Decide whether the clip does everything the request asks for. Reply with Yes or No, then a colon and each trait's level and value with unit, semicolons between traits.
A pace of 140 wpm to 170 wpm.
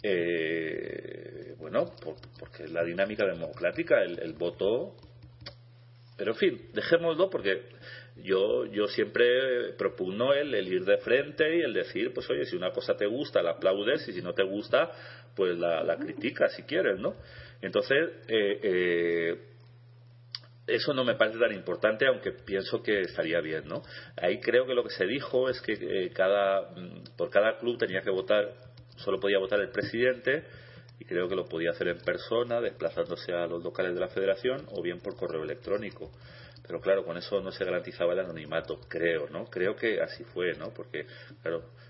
No: average, 180 wpm